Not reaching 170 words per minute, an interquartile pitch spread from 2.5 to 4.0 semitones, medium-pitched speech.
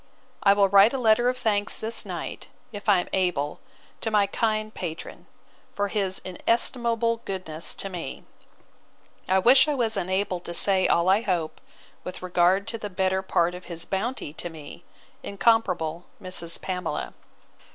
No: average, 160 wpm; average, 3.5 semitones; high, 195 Hz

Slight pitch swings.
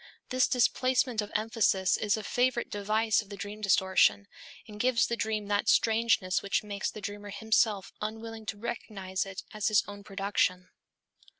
Yes: narrow, 2.0 semitones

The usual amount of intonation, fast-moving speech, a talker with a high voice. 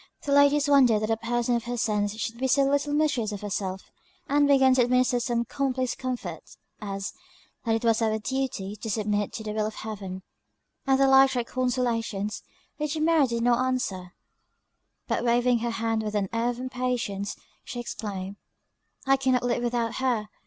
No: average, 3.2 semitones; average, 185 wpm; high, 240 Hz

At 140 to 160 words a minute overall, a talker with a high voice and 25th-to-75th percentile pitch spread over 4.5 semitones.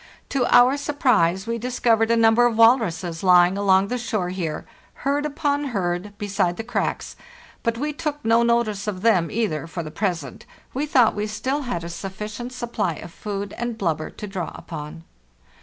No: average, 175 wpm; high, 215 Hz; average, 5.1 semitones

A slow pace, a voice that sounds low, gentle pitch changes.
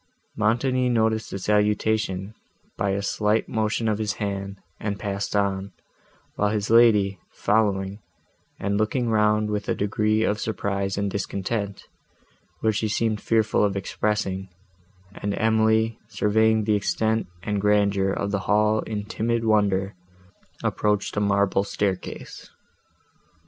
Yes: slow, 130 wpm; low, 105 Hz; narrow, 1.6 semitones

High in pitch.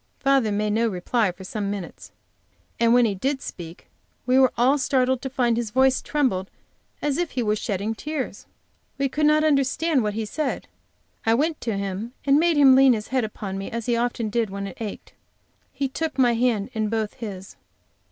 Yes: high, 235 Hz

